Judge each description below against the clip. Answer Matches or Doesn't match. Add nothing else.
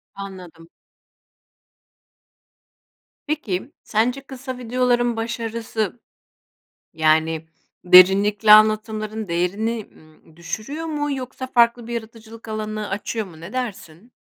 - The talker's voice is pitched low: Doesn't match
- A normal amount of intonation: Matches